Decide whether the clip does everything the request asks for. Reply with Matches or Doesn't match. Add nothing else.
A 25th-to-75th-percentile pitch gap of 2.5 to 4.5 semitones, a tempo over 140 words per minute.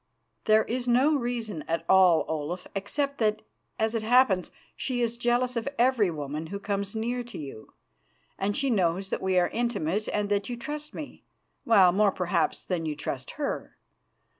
Doesn't match